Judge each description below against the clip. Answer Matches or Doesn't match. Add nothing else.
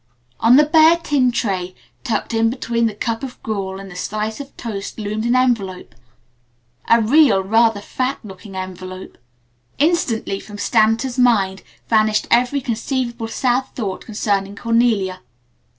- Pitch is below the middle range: Doesn't match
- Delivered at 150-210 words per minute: Doesn't match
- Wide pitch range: Doesn't match